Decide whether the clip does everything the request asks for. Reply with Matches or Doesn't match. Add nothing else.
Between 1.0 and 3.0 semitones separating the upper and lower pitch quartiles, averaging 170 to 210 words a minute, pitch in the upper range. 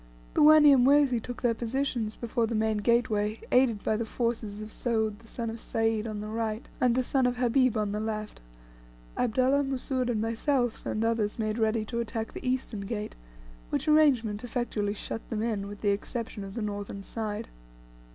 Matches